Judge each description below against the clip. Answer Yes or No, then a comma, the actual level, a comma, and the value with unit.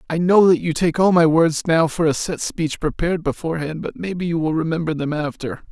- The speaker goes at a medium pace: No, fast, 230 wpm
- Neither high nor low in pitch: Yes, medium, 165 Hz